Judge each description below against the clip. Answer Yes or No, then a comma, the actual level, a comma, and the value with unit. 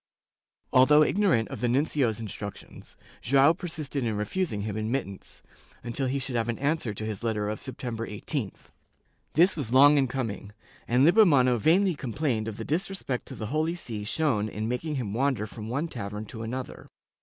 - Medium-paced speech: Yes, average, 180 wpm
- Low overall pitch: Yes, low, 125 Hz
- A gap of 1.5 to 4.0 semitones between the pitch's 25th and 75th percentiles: No, average, 5.2 semitones